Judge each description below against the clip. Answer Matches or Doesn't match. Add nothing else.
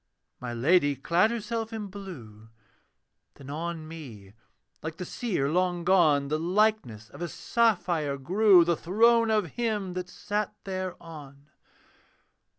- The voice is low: Doesn't match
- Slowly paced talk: Matches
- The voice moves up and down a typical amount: Doesn't match